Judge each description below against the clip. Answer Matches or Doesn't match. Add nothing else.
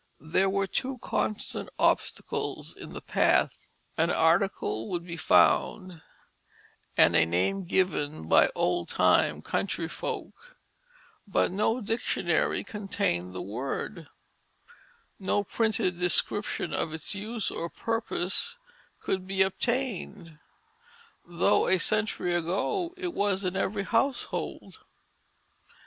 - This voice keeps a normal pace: Doesn't match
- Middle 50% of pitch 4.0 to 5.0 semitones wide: Matches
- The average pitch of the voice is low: Doesn't match